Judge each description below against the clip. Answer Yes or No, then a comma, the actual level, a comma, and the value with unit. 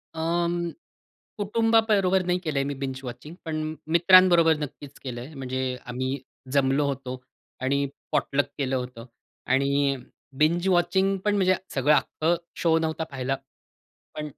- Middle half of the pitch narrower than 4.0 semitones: No, average, 4.5 semitones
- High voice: No, medium, 150 Hz